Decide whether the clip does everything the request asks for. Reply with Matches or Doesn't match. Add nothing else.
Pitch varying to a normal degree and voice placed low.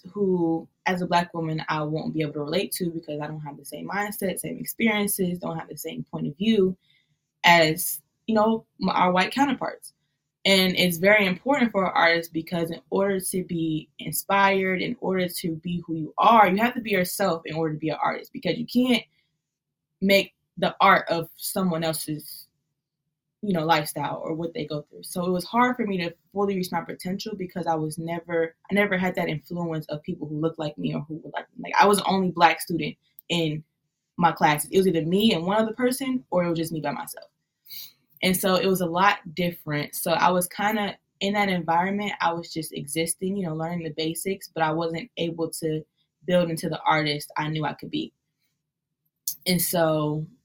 Doesn't match